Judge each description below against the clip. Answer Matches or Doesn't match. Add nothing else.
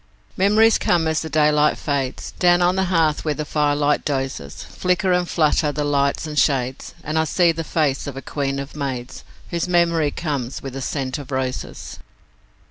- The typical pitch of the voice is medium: Matches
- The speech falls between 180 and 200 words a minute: Matches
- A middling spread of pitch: Matches